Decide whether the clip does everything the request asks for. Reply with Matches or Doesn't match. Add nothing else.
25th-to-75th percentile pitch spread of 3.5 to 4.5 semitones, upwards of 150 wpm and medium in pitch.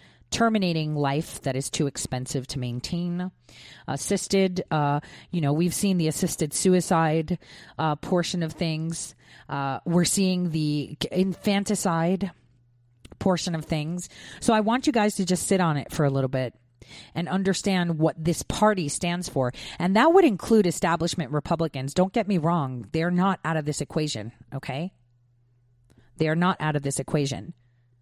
Doesn't match